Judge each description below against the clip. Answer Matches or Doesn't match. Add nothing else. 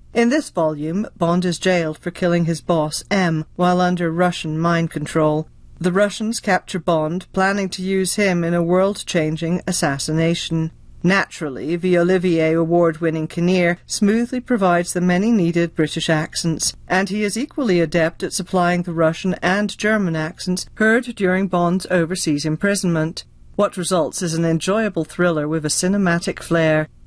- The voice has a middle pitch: Matches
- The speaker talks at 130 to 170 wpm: Matches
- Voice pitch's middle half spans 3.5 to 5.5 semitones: Doesn't match